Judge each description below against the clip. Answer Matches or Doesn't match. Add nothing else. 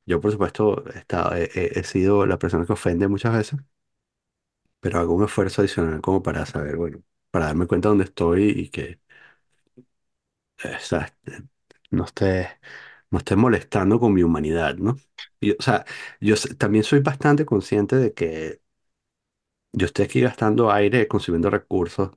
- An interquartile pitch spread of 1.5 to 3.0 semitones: Doesn't match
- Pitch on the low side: Matches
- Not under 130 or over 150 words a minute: Doesn't match